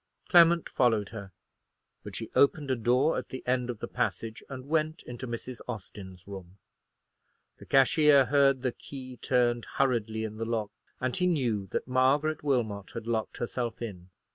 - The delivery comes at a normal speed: Yes, average, 165 wpm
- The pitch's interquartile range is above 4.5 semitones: No, average, 3.7 semitones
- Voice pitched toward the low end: Yes, low, 125 Hz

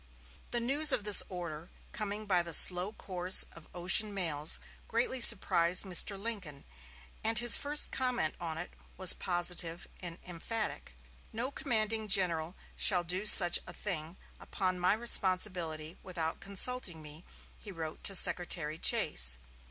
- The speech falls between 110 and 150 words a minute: Yes, average, 140 wpm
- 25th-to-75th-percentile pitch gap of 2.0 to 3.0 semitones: No, average, 4.2 semitones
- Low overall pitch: No, medium, 185 Hz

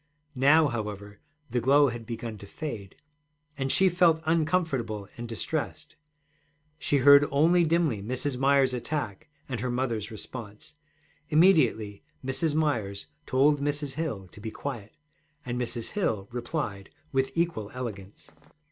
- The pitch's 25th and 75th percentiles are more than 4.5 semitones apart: Yes, wide, 5.6 semitones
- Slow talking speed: Yes, slow, 130 wpm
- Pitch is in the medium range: No, low, 130 Hz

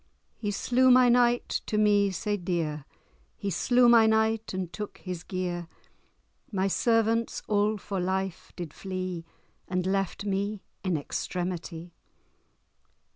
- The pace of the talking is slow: Yes, slow, 130 wpm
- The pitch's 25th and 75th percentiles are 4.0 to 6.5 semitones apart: No, average, 3.4 semitones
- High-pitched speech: Yes, high, 195 Hz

